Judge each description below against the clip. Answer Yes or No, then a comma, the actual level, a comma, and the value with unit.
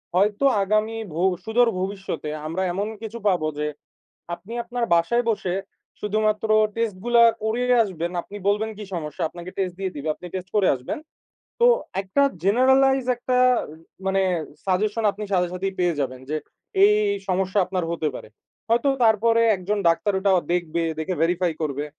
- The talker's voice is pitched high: Yes, high, 195 Hz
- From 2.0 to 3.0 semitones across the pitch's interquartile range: No, average, 3.9 semitones